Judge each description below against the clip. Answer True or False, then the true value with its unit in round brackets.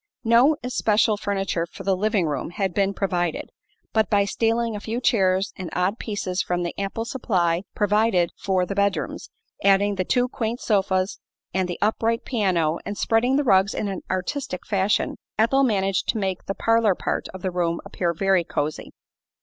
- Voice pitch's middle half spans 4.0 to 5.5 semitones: False (3.2 semitones)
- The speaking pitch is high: True (195 Hz)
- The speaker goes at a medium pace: True (175 wpm)